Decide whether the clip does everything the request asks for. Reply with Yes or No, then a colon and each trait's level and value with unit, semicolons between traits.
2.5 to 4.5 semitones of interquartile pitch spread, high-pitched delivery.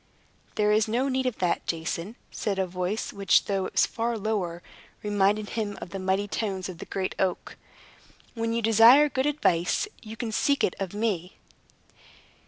Yes: average, 3.4 semitones; high, 210 Hz